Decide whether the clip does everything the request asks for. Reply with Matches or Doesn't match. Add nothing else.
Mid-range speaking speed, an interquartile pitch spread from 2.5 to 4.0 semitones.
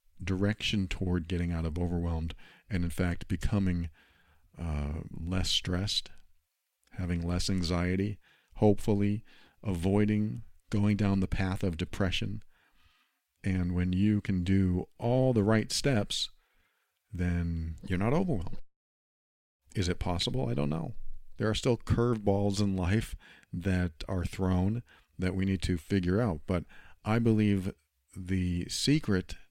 Doesn't match